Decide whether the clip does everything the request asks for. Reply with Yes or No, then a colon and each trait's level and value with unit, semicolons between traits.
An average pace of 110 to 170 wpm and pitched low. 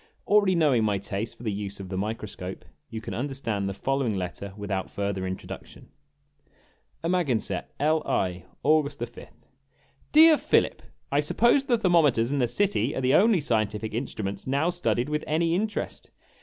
Yes: average, 160 wpm; low, 120 Hz